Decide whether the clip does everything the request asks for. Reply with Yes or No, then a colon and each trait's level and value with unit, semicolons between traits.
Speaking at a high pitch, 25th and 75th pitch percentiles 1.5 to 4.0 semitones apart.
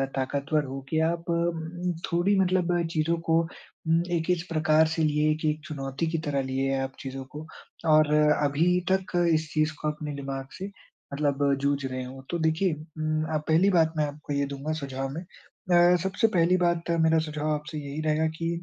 No: medium, 155 Hz; average, 2.7 semitones